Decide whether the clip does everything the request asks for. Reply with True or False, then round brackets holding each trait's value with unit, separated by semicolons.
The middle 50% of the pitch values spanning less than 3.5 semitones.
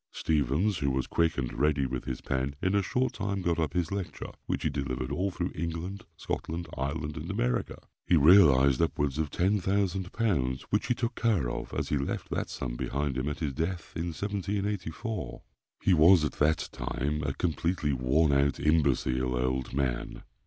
False (5.3 semitones)